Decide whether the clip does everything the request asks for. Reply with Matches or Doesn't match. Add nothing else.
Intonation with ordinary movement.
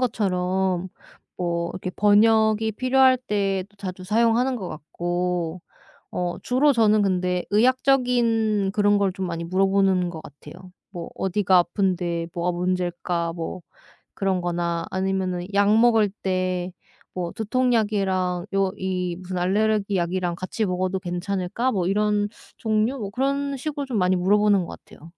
Matches